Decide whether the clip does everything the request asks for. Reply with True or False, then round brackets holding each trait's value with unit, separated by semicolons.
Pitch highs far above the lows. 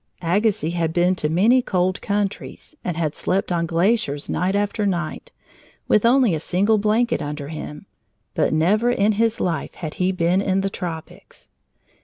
False (4.0 semitones)